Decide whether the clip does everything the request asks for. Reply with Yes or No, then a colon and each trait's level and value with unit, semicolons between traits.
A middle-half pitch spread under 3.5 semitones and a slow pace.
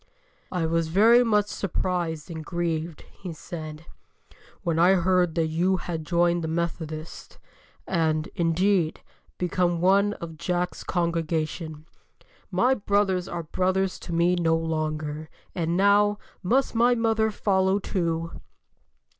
Yes: average, 2.8 semitones; slow, 125 wpm